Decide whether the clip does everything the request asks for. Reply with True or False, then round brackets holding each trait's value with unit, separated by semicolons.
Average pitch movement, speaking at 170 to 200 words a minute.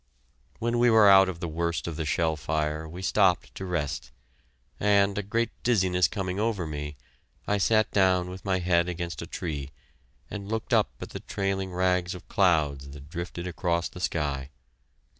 True (3.4 semitones; 180 wpm)